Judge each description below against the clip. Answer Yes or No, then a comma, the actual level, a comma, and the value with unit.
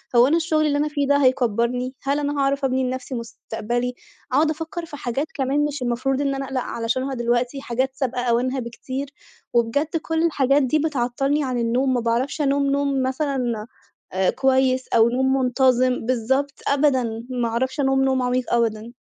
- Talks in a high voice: Yes, very high, 260 Hz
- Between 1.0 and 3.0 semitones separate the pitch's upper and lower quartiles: Yes, narrow, 2.6 semitones